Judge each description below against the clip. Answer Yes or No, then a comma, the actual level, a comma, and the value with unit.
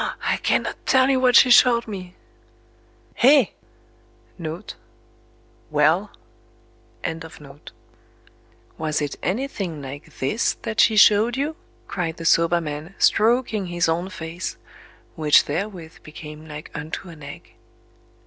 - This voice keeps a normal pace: No, slow, 110 wpm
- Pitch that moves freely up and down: Yes, wide, 6.1 semitones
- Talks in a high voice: No, medium, 175 Hz